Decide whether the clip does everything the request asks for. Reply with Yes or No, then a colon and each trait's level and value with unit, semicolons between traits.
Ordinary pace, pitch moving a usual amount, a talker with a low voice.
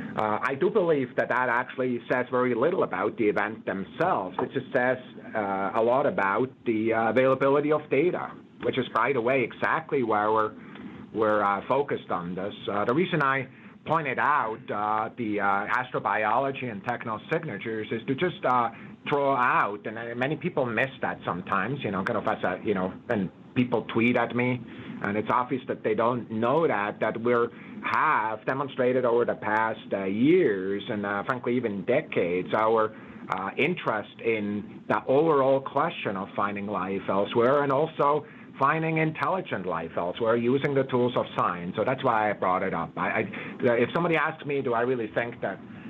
Yes: average, 180 wpm; average, 3.7 semitones; low, 120 Hz